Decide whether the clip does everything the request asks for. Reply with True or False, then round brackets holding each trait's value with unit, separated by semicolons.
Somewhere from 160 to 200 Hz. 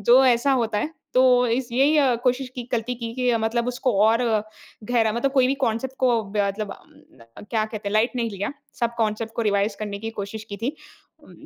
False (230 Hz)